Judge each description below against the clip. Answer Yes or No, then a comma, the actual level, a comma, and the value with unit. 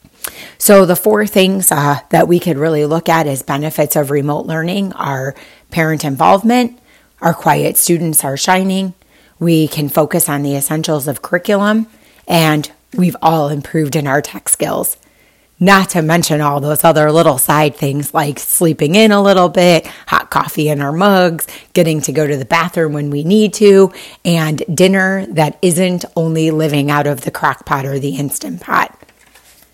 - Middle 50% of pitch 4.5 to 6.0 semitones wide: No, average, 3.7 semitones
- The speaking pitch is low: No, medium, 160 Hz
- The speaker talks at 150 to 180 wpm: Yes, average, 170 wpm